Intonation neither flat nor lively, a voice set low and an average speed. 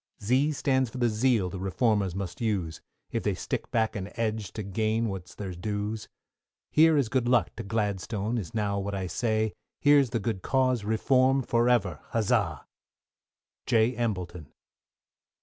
Yes: average, 3.5 semitones; low, 110 Hz; average, 160 wpm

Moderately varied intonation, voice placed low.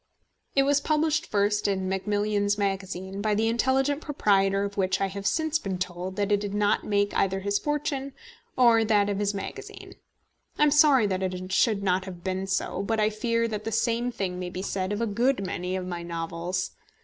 No: average, 3.4 semitones; high, 205 Hz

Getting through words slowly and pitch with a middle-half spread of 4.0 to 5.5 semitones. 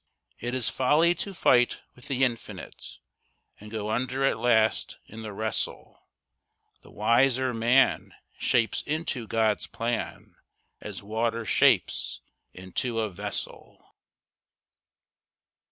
No: slow, 110 wpm; average, 2.7 semitones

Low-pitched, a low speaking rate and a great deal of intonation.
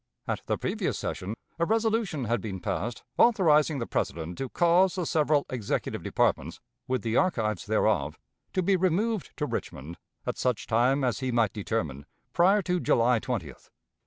No: low, 130 Hz; average, 160 wpm; wide, 8.1 semitones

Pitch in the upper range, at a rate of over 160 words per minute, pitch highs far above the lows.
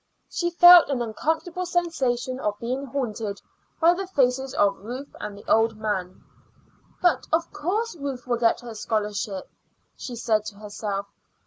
No: high, 245 Hz; average, 150 wpm; wide, 7.1 semitones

